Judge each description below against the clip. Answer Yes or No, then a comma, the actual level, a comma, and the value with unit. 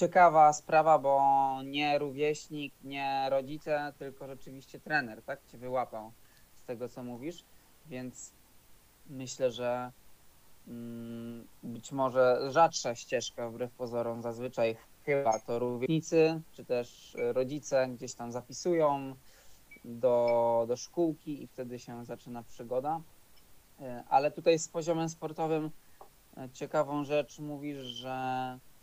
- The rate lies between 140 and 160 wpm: No, slow, 110 wpm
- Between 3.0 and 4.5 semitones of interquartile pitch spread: Yes, average, 3.5 semitones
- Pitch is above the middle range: No, low, 135 Hz